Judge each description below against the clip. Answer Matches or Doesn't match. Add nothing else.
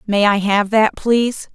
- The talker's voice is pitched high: Matches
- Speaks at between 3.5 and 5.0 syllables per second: Matches